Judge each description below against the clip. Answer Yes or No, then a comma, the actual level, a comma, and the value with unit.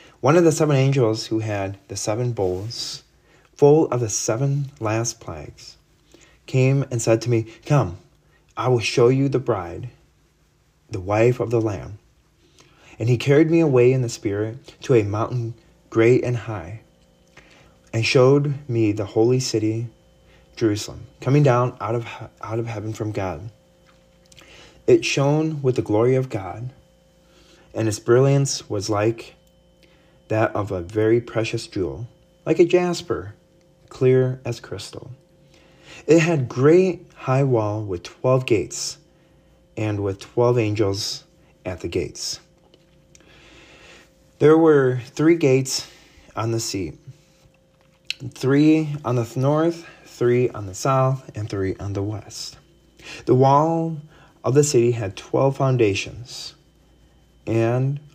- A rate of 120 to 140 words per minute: Yes, slow, 135 wpm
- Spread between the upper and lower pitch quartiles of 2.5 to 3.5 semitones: No, average, 4.9 semitones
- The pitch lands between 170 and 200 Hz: No, low, 125 Hz